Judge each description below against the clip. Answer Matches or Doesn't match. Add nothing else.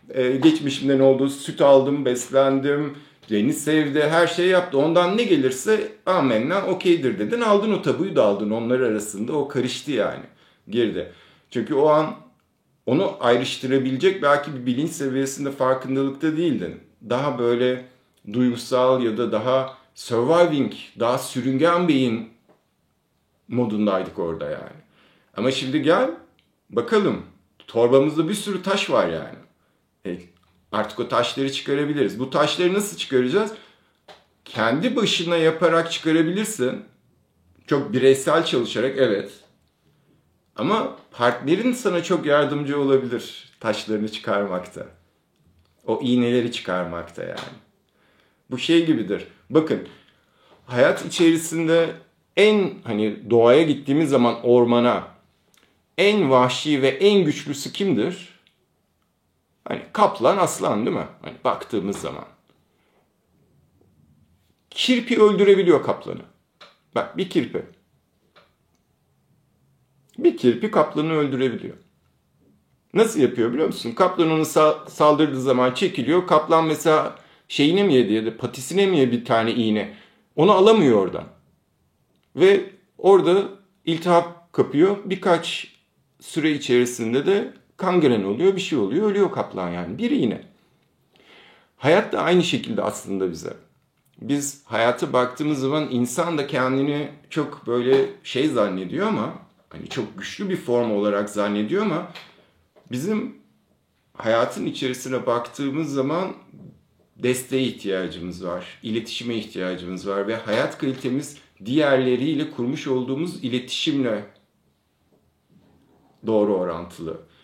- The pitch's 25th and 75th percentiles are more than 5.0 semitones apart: Matches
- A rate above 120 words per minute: Doesn't match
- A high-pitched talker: Doesn't match